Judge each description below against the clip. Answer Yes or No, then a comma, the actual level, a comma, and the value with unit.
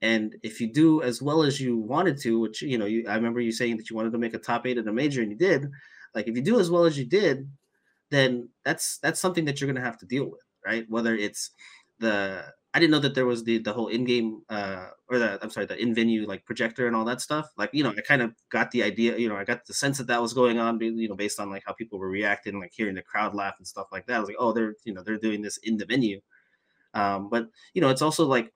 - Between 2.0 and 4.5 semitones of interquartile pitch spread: Yes, average, 2.9 semitones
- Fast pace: Yes, fast, 290 wpm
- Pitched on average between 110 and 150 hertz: Yes, low, 115 Hz